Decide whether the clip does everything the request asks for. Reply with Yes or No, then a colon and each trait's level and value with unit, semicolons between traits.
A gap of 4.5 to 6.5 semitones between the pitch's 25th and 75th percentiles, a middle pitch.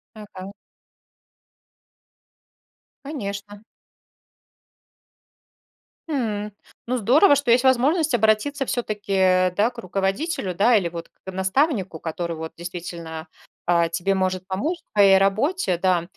No: average, 5.0 semitones; high, 200 Hz